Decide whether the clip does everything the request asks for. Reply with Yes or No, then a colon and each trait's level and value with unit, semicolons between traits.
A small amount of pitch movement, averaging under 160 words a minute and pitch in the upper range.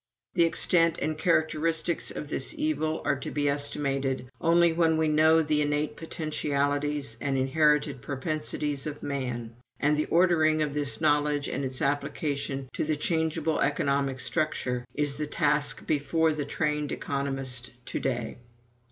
No: narrow, 2.2 semitones; average, 145 wpm; medium, 150 Hz